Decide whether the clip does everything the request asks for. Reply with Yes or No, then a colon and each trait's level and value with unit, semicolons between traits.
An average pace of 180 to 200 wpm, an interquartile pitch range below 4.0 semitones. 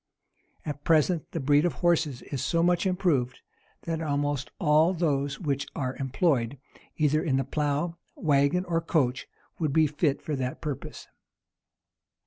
No: average, 150 wpm; average, 3.2 semitones